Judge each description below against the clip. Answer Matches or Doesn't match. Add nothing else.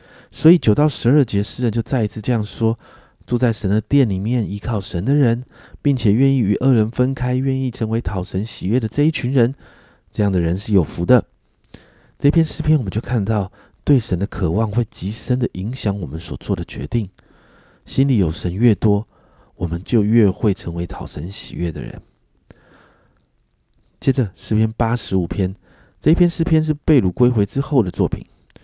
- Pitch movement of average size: Matches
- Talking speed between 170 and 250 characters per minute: Doesn't match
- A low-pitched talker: Matches